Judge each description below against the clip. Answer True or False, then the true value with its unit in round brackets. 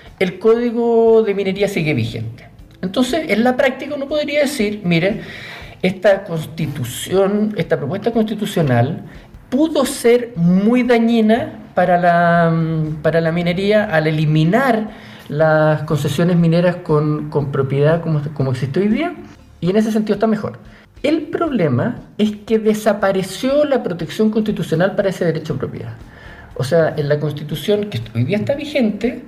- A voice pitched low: False (190 Hz)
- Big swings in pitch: True (6.3 semitones)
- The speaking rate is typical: True (145 wpm)